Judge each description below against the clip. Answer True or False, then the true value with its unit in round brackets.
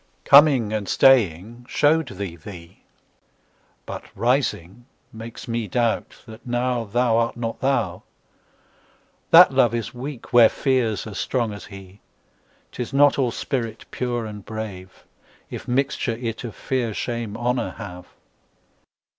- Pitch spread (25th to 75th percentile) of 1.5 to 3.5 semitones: True (3.1 semitones)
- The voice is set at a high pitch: False (115 Hz)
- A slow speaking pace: True (115 wpm)